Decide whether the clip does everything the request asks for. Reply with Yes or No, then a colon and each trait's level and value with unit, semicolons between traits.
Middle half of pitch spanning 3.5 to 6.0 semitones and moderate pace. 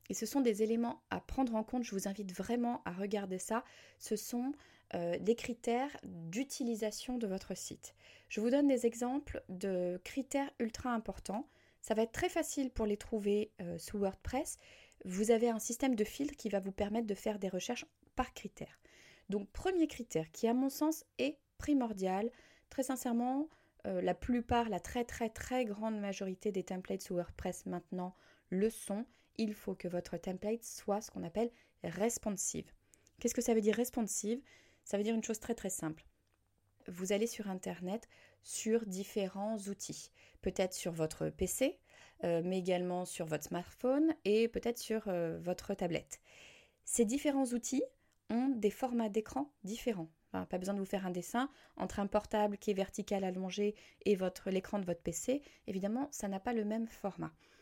Yes: average, 4.1 semitones; average, 180 wpm